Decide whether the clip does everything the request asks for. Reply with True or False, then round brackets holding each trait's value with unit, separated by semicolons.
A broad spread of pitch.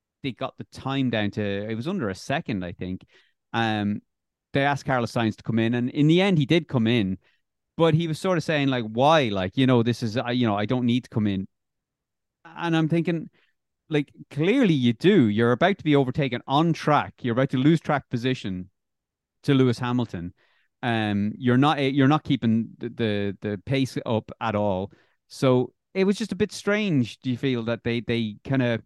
False (4.5 semitones)